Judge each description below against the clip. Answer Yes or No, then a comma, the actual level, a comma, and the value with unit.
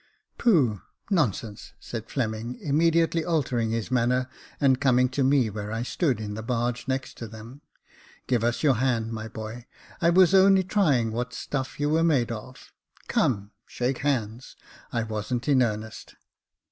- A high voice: No, low, 125 Hz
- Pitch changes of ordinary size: Yes, average, 4.2 semitones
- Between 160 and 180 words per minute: Yes, average, 170 wpm